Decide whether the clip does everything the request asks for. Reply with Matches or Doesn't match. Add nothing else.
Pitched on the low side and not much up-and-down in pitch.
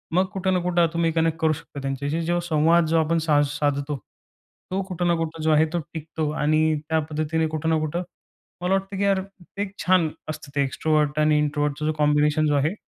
Doesn't match